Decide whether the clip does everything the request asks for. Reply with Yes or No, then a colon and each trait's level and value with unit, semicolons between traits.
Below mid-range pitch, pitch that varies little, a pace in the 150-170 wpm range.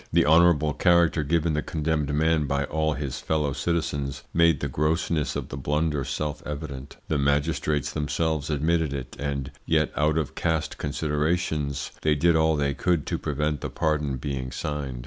Yes: very low, 75 Hz; narrow, 2.0 semitones; average, 165 wpm